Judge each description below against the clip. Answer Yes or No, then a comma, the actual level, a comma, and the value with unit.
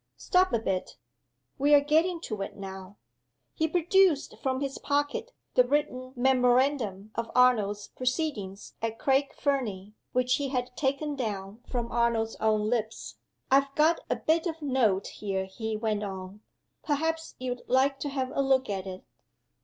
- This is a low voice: No, very high, 250 Hz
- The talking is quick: No, average, 155 wpm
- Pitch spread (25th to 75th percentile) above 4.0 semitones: Yes, average, 5.1 semitones